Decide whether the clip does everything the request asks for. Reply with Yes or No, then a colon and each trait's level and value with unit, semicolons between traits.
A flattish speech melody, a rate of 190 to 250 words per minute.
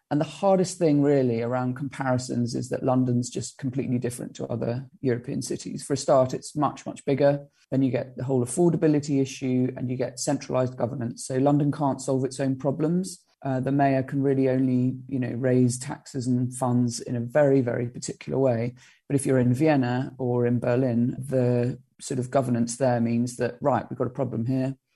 Yes: narrow, 2.0 semitones; average, 195 wpm